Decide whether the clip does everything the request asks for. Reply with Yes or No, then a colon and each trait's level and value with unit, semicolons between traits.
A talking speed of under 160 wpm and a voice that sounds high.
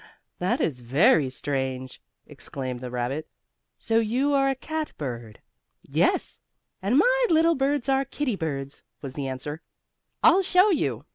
No: average, 145 wpm; medium, 160 Hz